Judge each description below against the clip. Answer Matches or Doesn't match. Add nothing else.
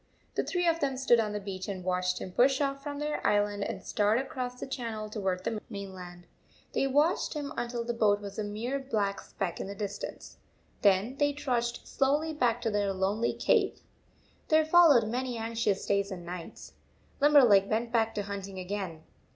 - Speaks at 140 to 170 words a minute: Doesn't match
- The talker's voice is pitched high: Matches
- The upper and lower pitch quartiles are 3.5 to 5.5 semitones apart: Matches